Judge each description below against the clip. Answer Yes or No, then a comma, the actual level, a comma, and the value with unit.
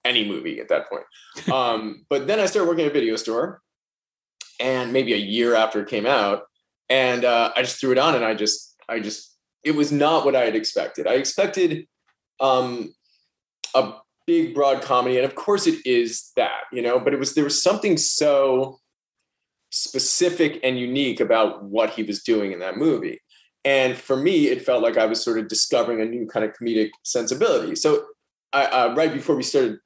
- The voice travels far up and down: Yes, wide, 7.0 semitones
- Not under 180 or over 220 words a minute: Yes, average, 200 wpm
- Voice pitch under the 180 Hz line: Yes, low, 135 Hz